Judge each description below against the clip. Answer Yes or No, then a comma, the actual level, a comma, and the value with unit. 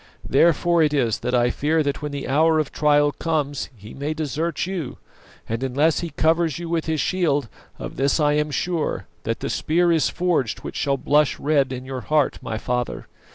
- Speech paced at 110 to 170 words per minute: No, average, 200 wpm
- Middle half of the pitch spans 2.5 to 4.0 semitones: Yes, average, 3.1 semitones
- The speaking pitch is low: No, medium, 150 Hz